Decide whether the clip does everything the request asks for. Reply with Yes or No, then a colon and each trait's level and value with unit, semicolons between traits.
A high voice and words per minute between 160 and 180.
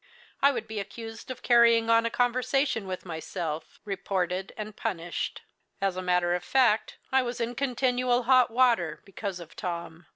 Yes: high, 220 Hz; average, 165 wpm